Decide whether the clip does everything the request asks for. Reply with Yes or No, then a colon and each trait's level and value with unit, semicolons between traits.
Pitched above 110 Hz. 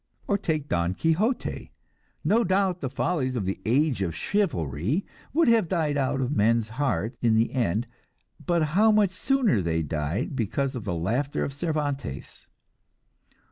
Yes: medium, 140 Hz